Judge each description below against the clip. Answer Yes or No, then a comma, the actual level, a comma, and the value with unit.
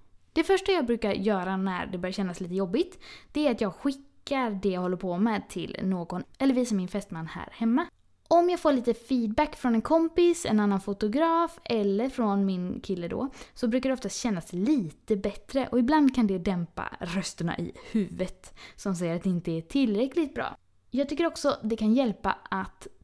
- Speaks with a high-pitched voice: Yes, high, 220 Hz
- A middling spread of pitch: No, wide, 6.2 semitones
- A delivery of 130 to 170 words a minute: No, fast, 195 wpm